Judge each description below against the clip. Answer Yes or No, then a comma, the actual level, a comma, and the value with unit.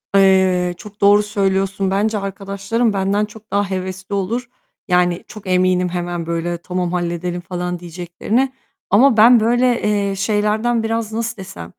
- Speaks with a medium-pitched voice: No, high, 195 Hz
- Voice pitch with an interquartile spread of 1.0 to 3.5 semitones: Yes, average, 3.0 semitones